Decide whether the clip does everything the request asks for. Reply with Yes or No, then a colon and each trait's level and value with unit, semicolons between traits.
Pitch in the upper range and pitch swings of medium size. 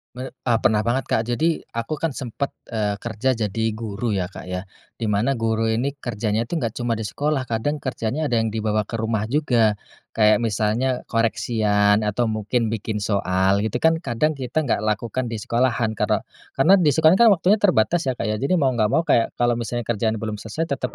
No: low, 115 Hz; average, 3.3 semitones